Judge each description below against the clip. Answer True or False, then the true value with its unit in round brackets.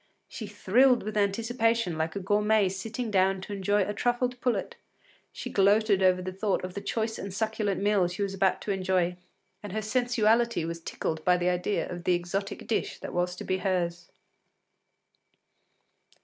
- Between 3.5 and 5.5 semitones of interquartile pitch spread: False (3.0 semitones)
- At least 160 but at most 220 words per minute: True (175 wpm)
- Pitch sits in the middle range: False (200 Hz)